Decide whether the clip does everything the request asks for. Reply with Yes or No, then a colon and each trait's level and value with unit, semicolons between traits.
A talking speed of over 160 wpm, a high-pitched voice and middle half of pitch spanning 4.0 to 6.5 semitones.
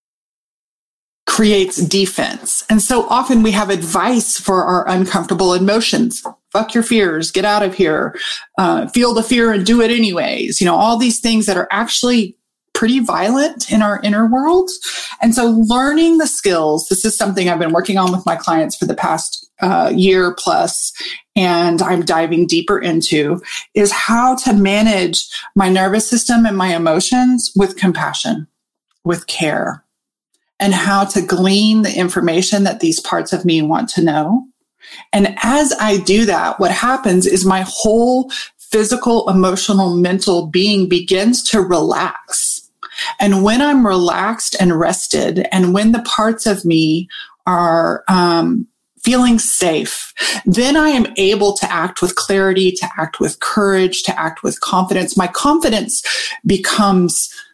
No: average, 155 wpm; high, 205 Hz; average, 4.3 semitones